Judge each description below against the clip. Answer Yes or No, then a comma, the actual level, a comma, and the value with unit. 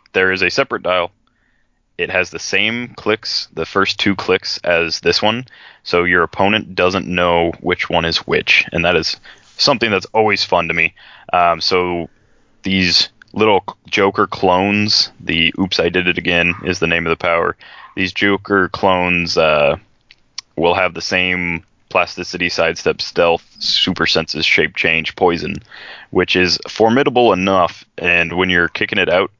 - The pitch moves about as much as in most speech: No, narrow, 2.0 semitones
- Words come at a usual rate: Yes, average, 160 wpm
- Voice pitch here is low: Yes, very low, 90 Hz